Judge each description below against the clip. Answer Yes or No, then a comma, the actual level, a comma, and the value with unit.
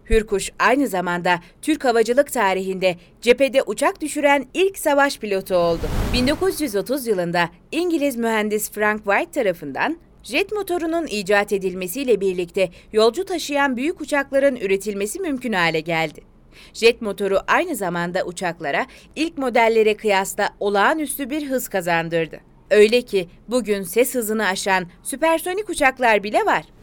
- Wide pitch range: Yes, wide, 6.7 semitones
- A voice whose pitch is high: Yes, high, 220 Hz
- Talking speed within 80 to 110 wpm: No, average, 125 wpm